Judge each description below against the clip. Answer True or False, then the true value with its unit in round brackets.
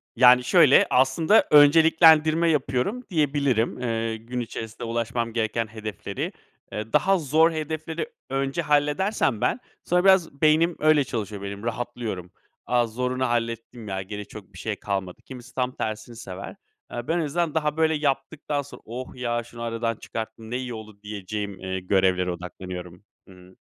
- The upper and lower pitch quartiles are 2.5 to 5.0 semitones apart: False (5.5 semitones)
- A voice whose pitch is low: True (120 Hz)